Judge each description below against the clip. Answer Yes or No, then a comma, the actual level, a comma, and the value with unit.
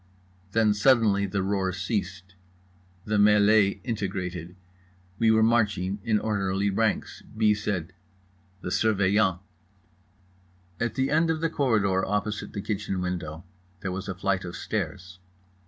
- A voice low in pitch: Yes, low, 100 Hz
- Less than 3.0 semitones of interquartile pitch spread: Yes, narrow, 2.6 semitones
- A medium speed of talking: No, slow, 130 wpm